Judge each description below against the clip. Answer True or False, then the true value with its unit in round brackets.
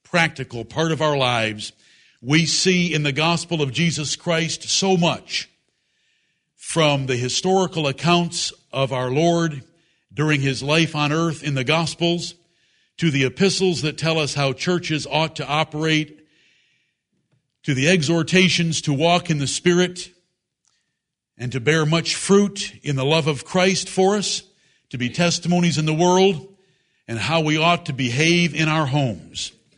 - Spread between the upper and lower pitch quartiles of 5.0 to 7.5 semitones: False (3.3 semitones)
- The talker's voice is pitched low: False (160 Hz)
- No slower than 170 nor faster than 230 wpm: False (155 wpm)